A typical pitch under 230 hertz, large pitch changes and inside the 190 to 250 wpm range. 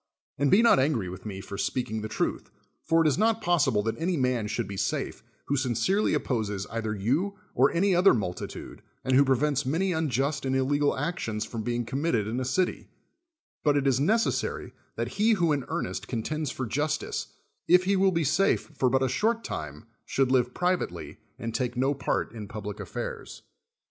Yes: low, 135 Hz; wide, 6.2 semitones; average, 195 wpm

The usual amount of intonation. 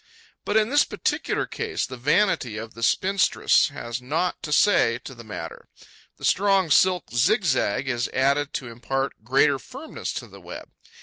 No: wide, 8.3 semitones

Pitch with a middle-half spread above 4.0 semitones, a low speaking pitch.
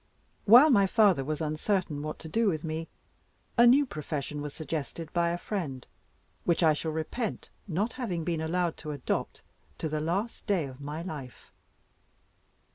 No: average, 4.5 semitones; medium, 165 Hz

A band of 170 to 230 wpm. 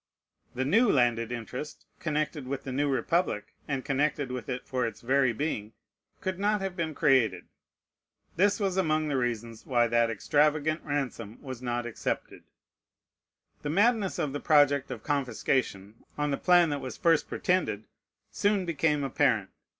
No: average, 155 wpm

